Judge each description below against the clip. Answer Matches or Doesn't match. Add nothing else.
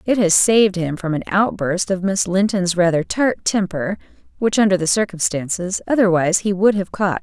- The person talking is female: Matches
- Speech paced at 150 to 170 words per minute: Doesn't match